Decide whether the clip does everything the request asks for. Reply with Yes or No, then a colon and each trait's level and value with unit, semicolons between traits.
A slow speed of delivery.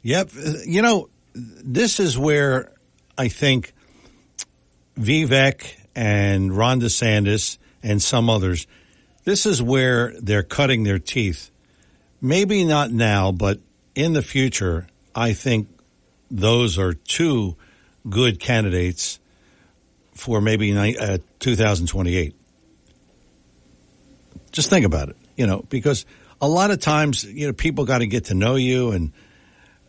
Yes: slow, 120 wpm